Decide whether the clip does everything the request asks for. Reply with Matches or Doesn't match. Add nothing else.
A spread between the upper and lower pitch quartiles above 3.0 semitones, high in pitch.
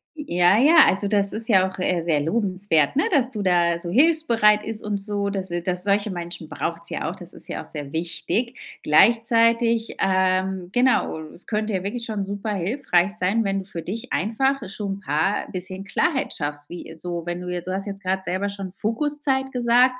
Matches